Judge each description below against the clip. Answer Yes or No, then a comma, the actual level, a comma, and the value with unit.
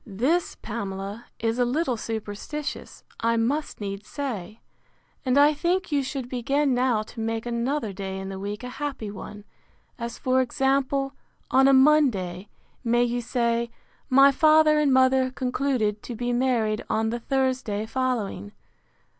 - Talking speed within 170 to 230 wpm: No, average, 150 wpm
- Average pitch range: Yes, average, 3.8 semitones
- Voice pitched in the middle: No, high, 245 Hz